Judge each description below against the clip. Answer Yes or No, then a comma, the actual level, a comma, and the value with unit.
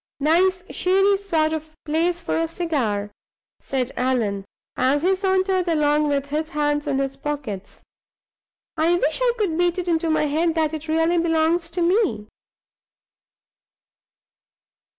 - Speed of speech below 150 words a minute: Yes, average, 140 wpm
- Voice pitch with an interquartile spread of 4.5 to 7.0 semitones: No, average, 3.2 semitones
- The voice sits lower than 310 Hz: No, very high, 320 Hz